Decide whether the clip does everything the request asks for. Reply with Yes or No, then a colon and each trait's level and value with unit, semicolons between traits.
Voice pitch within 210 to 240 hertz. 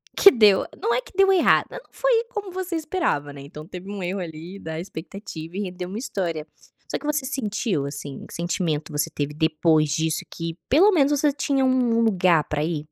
No: medium, 185 Hz